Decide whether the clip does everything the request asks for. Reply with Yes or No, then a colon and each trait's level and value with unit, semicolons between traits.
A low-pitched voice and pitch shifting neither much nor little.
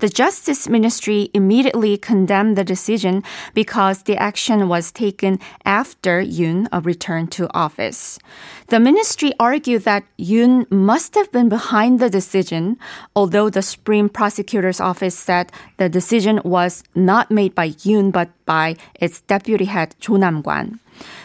No: high, 205 Hz; average, 3.5 semitones